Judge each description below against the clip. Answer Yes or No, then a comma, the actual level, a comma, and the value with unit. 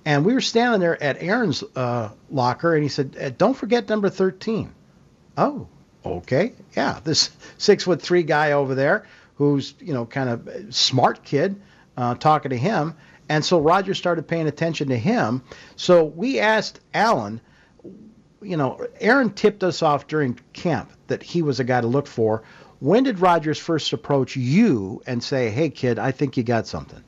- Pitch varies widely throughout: Yes, wide, 5.8 semitones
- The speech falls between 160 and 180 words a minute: Yes, average, 175 wpm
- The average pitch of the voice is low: No, medium, 150 Hz